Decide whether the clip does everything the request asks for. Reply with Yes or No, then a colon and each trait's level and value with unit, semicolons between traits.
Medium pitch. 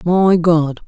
Yes: medium, 170 Hz